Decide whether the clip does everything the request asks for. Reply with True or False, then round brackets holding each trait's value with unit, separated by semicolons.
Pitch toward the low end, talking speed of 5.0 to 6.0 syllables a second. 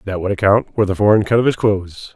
False (100 Hz; 6.7 syllables/s)